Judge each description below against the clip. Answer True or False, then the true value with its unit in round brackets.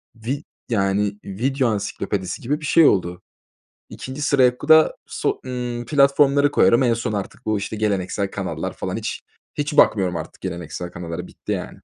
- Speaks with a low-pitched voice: True (115 Hz)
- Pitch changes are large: True (5.9 semitones)